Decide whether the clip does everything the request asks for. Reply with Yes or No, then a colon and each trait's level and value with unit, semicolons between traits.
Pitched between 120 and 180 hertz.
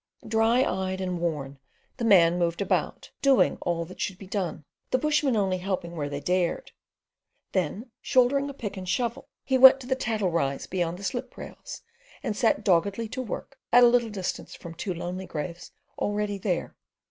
No: high, 195 Hz